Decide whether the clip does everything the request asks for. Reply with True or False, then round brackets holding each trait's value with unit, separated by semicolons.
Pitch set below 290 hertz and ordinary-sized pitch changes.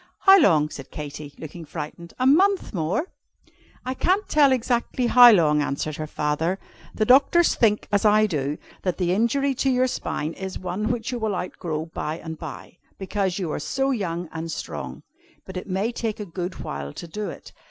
False (190 Hz; 7.2 semitones)